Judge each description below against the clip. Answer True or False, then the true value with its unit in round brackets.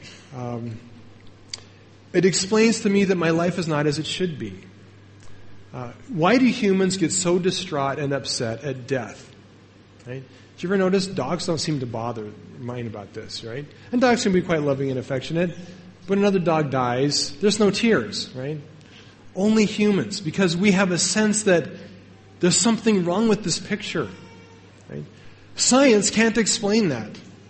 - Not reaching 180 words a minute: True (160 wpm)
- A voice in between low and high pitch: True (150 Hz)